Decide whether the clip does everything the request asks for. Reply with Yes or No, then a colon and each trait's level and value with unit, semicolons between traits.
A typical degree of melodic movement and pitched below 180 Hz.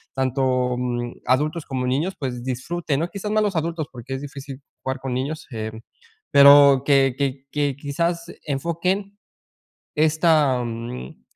Yes: average, 3.7 semitones; medium, 140 Hz